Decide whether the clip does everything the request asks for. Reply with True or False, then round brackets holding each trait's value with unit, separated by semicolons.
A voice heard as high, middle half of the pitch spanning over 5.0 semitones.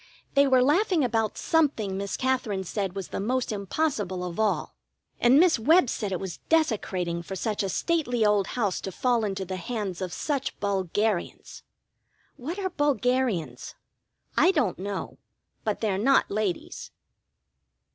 True (215 Hz; 5.4 semitones)